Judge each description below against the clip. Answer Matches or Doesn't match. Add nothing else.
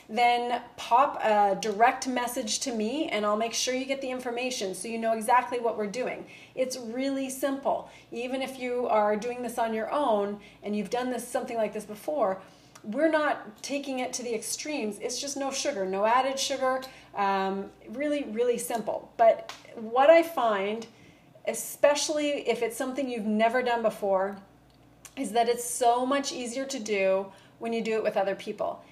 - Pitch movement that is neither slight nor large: Matches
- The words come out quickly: Doesn't match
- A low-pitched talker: Doesn't match